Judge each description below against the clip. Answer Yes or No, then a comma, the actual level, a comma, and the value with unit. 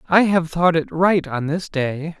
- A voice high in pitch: No, medium, 165 Hz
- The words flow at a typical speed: No, fast, 220 wpm